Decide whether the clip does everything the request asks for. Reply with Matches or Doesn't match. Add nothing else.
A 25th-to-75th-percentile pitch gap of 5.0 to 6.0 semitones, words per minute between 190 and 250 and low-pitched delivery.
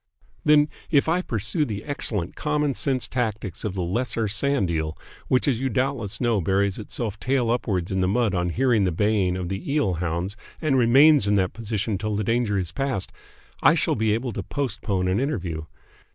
Matches